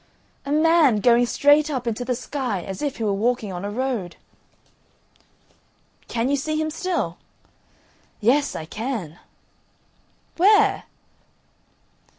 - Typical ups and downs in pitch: No, wide, 5.7 semitones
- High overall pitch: Yes, very high, 250 Hz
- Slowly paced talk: Yes, slow, 125 wpm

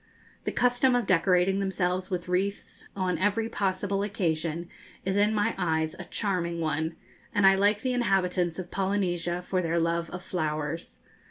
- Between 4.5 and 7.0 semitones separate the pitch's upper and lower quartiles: No, average, 2.9 semitones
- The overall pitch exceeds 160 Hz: Yes, medium, 185 Hz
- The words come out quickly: No, average, 160 wpm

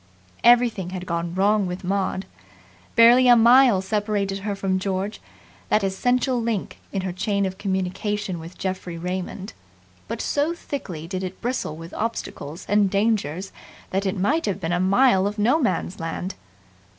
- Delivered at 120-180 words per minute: Yes, average, 160 wpm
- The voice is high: Yes, high, 195 Hz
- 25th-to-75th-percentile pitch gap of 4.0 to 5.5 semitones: No, average, 3.1 semitones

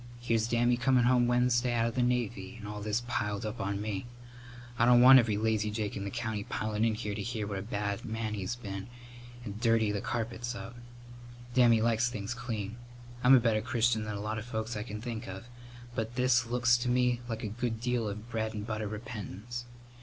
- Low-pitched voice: Yes, low, 115 Hz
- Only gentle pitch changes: Yes, narrow, 2.3 semitones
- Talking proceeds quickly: Yes, fast, 215 wpm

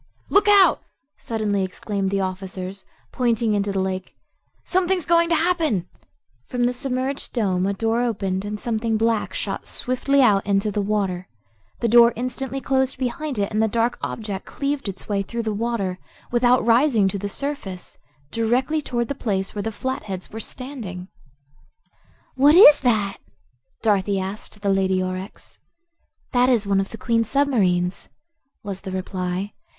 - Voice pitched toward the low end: No, high, 220 Hz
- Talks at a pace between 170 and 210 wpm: No, average, 155 wpm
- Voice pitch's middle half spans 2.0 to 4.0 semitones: No, average, 4.5 semitones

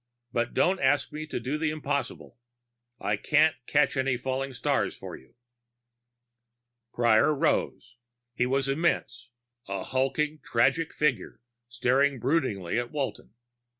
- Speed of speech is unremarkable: No, slow, 125 wpm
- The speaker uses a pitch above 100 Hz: Yes, low, 135 Hz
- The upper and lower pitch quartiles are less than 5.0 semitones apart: Yes, average, 3.6 semitones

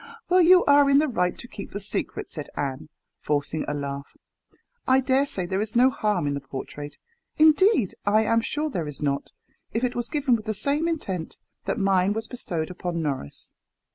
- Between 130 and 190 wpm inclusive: No, average, 200 wpm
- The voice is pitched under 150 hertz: No, high, 205 Hz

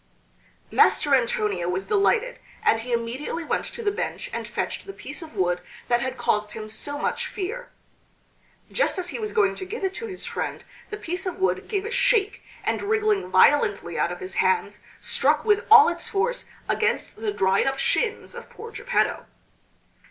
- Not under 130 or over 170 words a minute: No, average, 185 wpm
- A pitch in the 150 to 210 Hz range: No, very high, 385 Hz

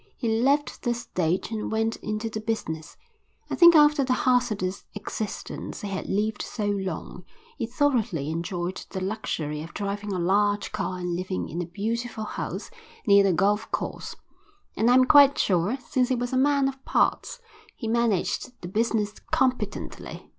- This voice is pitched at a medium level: No, high, 215 Hz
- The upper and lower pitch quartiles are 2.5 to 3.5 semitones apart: No, average, 4.5 semitones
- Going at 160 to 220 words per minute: Yes, average, 170 wpm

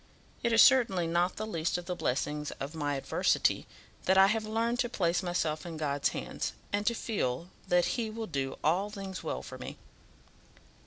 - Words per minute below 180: No, average, 190 wpm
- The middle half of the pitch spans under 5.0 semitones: No, wide, 5.5 semitones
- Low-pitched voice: No, medium, 180 Hz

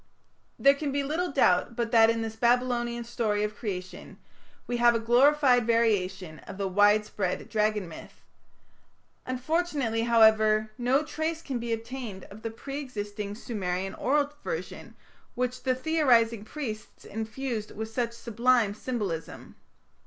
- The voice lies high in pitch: Yes, high, 230 Hz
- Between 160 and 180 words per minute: No, average, 140 wpm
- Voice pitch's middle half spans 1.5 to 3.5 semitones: Yes, average, 3.2 semitones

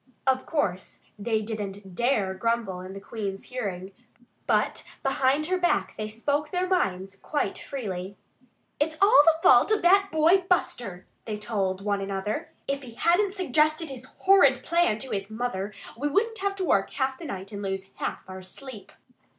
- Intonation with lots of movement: Yes, wide, 7.8 semitones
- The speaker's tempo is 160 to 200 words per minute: Yes, average, 170 wpm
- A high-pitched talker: Yes, high, 240 Hz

